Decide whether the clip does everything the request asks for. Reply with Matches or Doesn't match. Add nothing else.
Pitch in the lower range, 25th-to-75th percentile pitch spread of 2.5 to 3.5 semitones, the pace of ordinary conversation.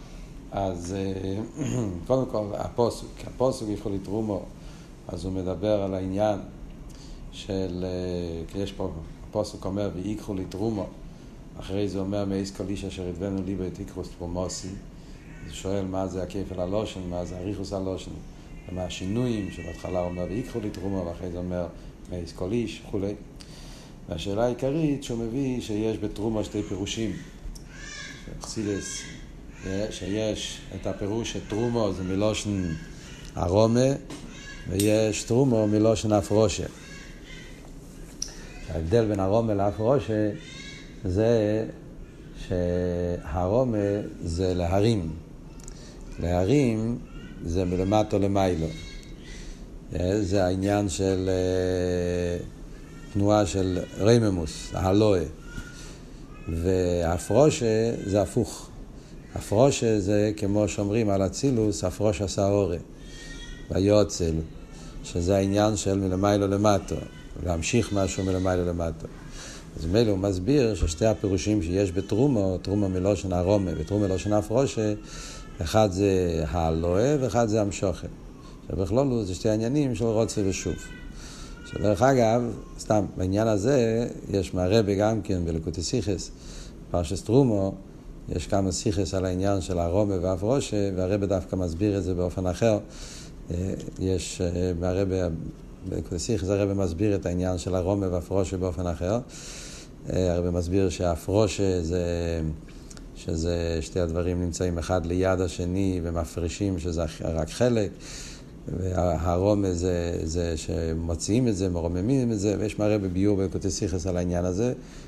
Matches